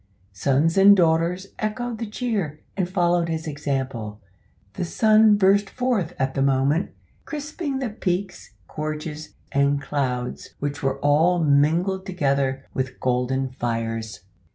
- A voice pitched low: No, medium, 160 Hz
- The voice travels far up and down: Yes, wide, 6.1 semitones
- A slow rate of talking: Yes, slow, 130 wpm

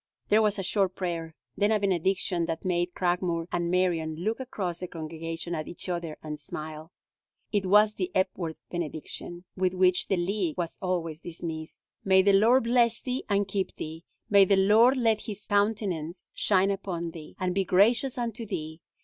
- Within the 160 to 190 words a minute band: Yes, average, 175 wpm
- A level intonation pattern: No, average, 3.3 semitones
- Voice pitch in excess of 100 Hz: Yes, medium, 185 Hz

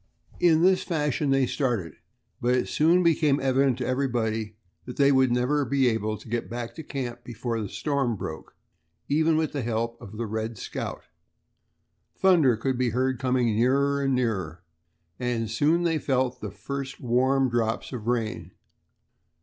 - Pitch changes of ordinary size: Yes, average, 3.3 semitones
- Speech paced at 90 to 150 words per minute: No, average, 165 wpm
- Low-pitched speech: Yes, low, 125 Hz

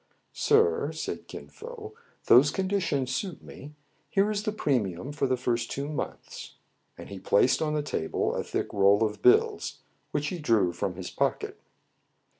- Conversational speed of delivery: Yes, average, 165 wpm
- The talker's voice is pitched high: No, medium, 140 Hz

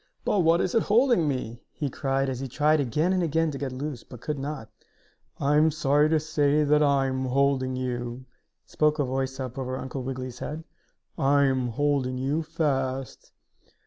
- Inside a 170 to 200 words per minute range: Yes, average, 180 wpm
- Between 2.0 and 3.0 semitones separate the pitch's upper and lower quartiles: Yes, average, 2.7 semitones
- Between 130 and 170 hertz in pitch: Yes, medium, 140 Hz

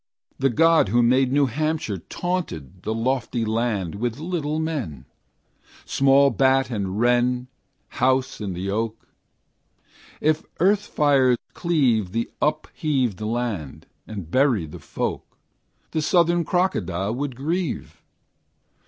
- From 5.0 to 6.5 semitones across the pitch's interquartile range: Yes, wide, 5.6 semitones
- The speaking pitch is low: Yes, low, 125 Hz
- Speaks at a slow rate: Yes, slow, 120 wpm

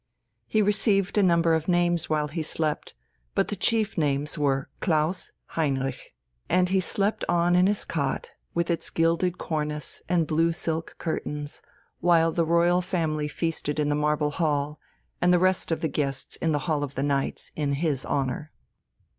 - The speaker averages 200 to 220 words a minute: No, average, 170 wpm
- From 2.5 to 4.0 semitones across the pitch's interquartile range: Yes, average, 2.9 semitones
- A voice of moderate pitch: Yes, medium, 160 Hz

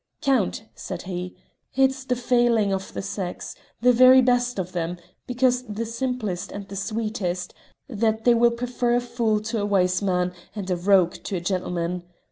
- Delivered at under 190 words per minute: Yes, average, 175 wpm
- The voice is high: Yes, high, 215 Hz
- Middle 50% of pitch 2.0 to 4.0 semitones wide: No, average, 4.9 semitones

